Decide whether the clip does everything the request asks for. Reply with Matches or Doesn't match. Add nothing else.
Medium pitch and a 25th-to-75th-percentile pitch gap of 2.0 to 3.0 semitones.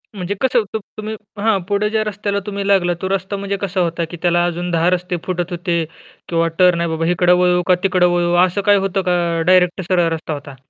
Matches